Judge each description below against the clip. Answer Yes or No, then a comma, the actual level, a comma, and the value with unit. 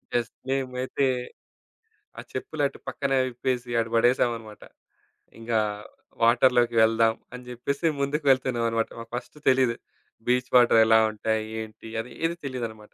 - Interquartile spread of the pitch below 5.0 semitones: Yes, narrow, 2.4 semitones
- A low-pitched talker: Yes, low, 120 Hz